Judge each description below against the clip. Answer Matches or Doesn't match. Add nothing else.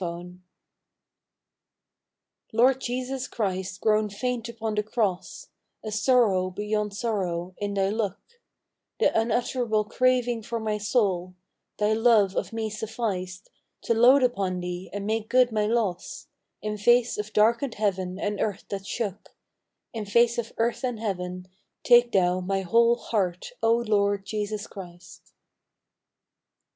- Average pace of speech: Doesn't match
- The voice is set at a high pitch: Matches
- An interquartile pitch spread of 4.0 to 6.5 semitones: Doesn't match